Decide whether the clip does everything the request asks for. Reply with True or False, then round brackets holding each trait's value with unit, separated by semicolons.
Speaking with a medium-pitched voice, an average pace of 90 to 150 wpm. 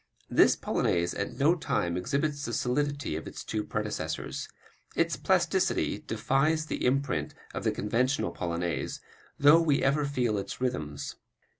False (125 Hz; 140 wpm)